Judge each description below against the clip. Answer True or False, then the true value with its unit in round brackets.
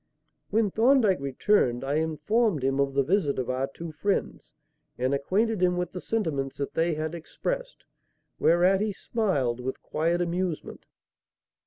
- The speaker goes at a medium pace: True (150 wpm)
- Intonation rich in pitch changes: True (6.5 semitones)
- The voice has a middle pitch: True (170 Hz)